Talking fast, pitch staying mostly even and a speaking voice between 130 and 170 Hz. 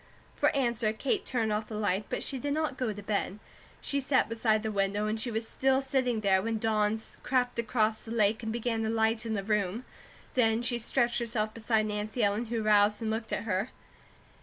No: fast, 210 wpm; narrow, 2.0 semitones; high, 220 Hz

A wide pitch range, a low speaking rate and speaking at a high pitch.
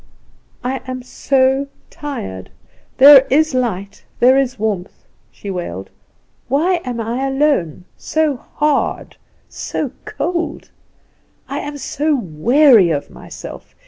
Yes: wide, 6.1 semitones; slow, 110 wpm; very high, 260 Hz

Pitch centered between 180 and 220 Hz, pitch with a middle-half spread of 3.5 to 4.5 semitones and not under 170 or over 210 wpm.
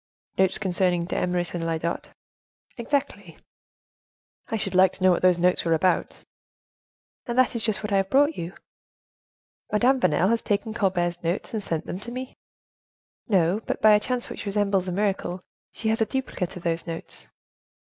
Yes: high, 190 Hz; average, 3.9 semitones; average, 175 wpm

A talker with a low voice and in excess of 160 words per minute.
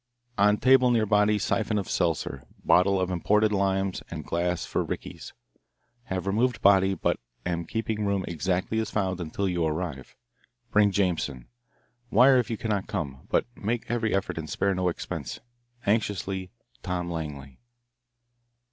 No: very low, 95 Hz; average, 145 wpm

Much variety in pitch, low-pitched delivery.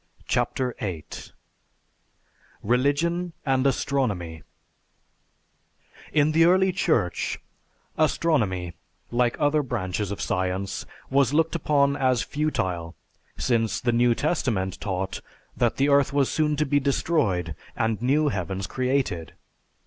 Yes: wide, 7.2 semitones; low, 130 Hz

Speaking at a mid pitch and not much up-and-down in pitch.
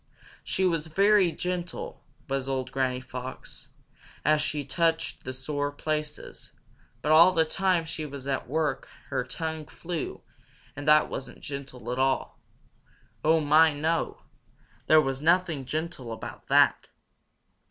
No: medium, 150 Hz; average, 3.4 semitones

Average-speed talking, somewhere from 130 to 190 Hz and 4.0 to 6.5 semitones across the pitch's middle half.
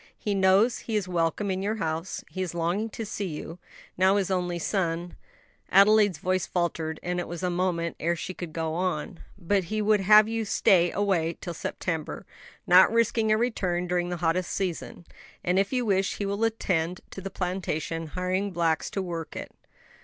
No: average, 190 wpm; medium, 185 Hz; average, 2.8 semitones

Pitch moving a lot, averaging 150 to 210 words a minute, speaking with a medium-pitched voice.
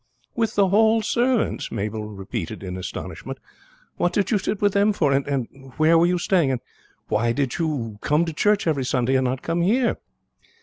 Yes: wide, 8.0 semitones; average, 190 wpm; medium, 160 Hz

